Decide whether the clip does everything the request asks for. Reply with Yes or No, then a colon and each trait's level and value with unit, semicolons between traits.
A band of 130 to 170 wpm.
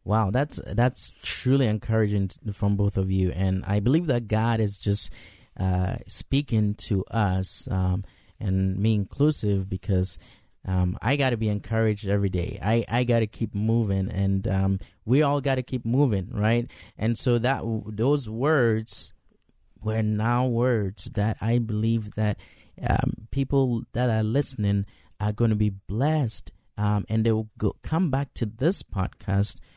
Yes: average, 165 wpm